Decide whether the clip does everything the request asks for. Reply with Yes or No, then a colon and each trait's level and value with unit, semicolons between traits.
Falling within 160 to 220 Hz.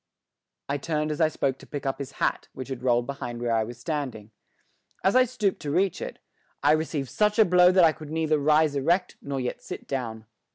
No: medium, 145 Hz